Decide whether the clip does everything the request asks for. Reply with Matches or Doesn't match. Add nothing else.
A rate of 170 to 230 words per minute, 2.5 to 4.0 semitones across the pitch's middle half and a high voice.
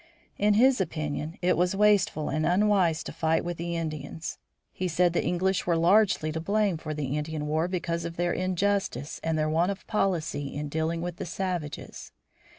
Doesn't match